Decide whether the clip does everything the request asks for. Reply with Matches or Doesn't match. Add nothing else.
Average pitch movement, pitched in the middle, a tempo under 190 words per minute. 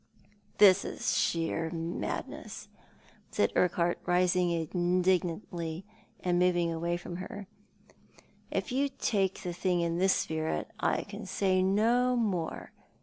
Doesn't match